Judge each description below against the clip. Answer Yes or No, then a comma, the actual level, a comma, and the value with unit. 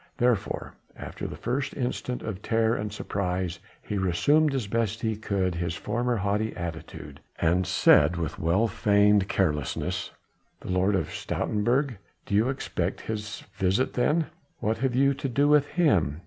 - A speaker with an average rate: Yes, average, 155 wpm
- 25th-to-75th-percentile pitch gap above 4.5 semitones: Yes, average, 5.0 semitones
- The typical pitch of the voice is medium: No, low, 105 Hz